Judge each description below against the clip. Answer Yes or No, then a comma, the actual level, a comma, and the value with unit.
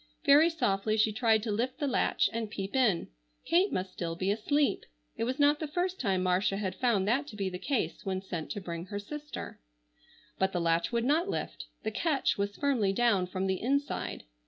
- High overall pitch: Yes, high, 215 Hz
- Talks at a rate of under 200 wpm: No, fast, 205 wpm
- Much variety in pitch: Yes, wide, 6.6 semitones